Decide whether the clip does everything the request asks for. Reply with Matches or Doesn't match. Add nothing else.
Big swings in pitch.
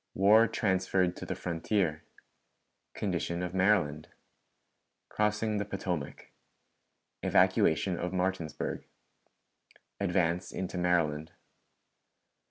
Doesn't match